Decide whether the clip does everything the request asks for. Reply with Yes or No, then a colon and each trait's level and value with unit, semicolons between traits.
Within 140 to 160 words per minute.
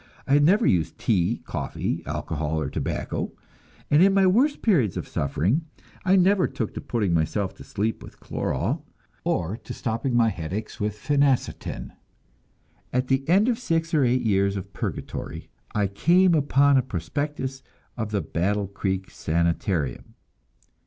Yes: average, 150 wpm